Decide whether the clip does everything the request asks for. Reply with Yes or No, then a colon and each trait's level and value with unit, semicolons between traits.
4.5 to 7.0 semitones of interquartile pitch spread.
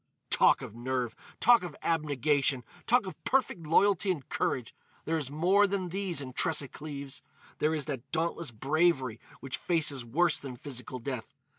Yes: average, 4.8 semitones